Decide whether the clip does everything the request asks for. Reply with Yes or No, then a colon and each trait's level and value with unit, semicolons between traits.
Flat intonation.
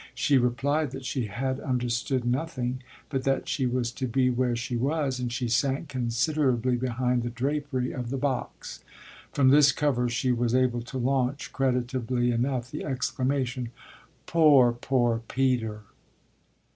Yes: narrow, 1.9 semitones